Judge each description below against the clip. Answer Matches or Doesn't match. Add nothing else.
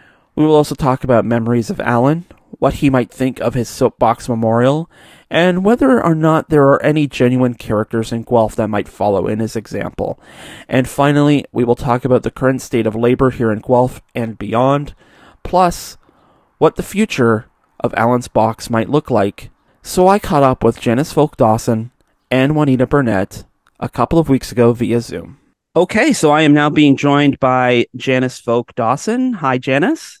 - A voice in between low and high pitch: Doesn't match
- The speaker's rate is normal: Matches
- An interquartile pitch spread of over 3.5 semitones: Matches